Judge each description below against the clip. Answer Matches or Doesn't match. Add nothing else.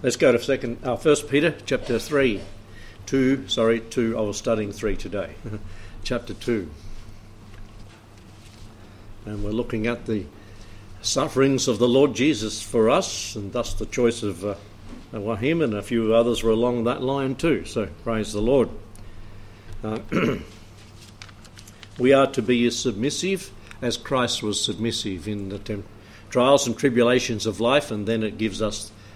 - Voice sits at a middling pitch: Doesn't match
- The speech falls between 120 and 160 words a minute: Matches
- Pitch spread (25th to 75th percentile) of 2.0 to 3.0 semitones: Matches